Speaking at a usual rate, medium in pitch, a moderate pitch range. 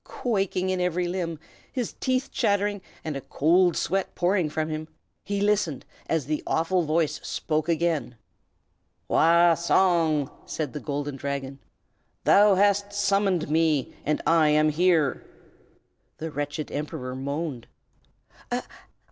No: slow, 125 wpm; medium, 165 Hz; average, 3.9 semitones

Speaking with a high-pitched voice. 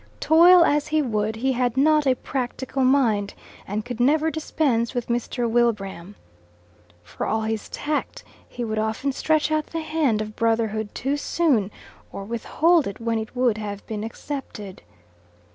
Yes: high, 240 Hz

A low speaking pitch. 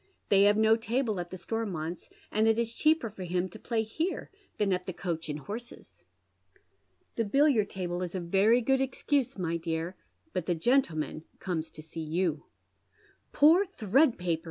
No: high, 195 Hz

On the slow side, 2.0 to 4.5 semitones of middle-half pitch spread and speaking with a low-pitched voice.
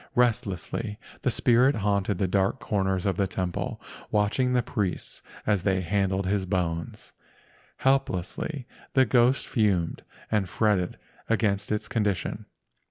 Yes: slow, 125 wpm; average, 3.4 semitones; low, 100 Hz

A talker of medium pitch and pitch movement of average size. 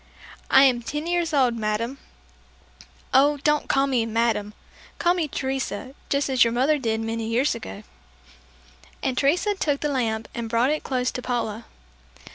No: very high, 255 Hz; average, 3.9 semitones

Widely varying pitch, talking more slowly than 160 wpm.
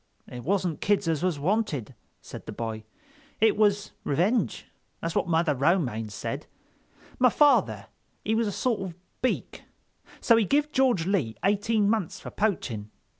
Yes: wide, 6.6 semitones; average, 150 wpm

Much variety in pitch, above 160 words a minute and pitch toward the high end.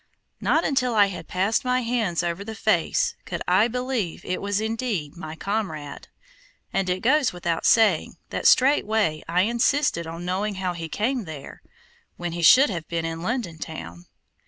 Yes: wide, 5.7 semitones; average, 170 wpm; high, 195 Hz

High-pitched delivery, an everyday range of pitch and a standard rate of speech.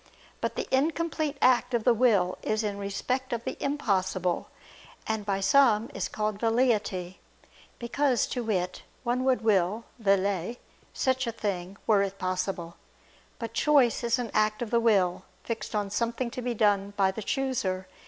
Yes: high, 220 Hz; average, 3.9 semitones; average, 165 wpm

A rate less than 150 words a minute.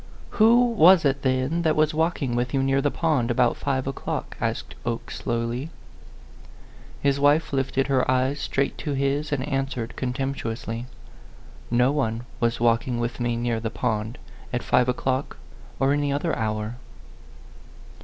No: average, 155 wpm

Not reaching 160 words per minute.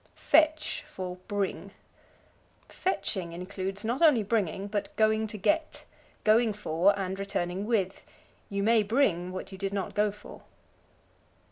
Yes: slow, 135 wpm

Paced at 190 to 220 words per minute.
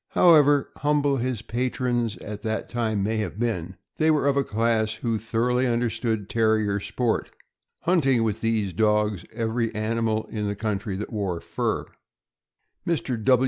No: average, 155 wpm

